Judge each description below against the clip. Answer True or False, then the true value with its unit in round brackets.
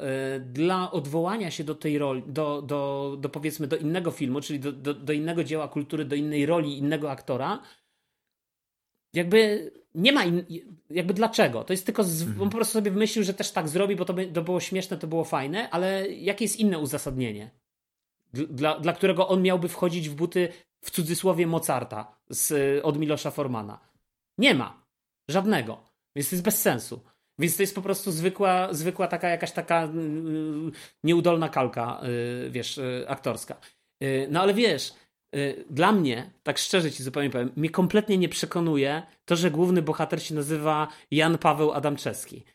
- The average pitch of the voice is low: False (160 Hz)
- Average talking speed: False (165 wpm)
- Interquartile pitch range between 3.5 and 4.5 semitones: True (4.1 semitones)